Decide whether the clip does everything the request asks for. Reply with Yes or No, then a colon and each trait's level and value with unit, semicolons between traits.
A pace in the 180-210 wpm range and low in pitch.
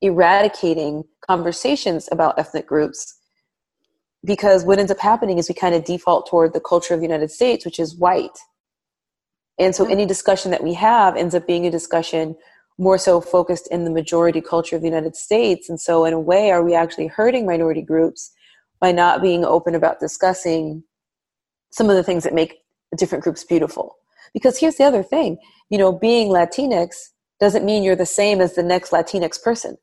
No: average, 190 wpm; medium, 175 Hz